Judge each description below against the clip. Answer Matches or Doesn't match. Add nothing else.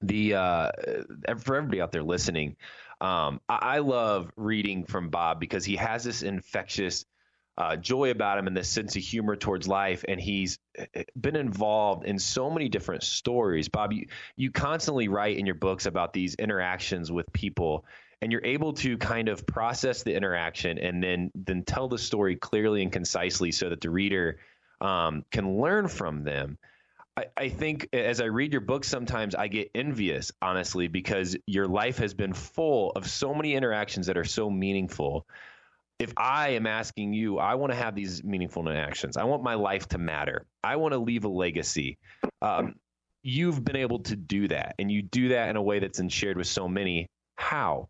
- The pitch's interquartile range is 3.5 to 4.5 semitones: Matches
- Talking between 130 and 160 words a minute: Doesn't match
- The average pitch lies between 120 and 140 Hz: Doesn't match